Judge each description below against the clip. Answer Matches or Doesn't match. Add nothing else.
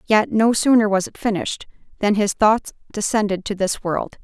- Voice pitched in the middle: Doesn't match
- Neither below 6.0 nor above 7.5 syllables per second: Doesn't match